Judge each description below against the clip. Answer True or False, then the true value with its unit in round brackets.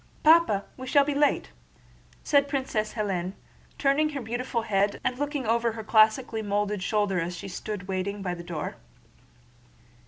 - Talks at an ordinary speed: True (155 wpm)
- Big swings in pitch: False (5.0 semitones)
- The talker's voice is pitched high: True (220 Hz)